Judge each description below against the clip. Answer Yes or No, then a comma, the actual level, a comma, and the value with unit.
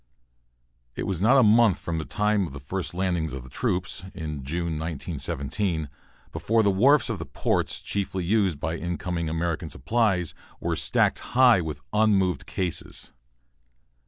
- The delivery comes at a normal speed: Yes, average, 150 wpm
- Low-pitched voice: Yes, very low, 90 Hz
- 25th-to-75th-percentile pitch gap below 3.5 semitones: No, average, 4.6 semitones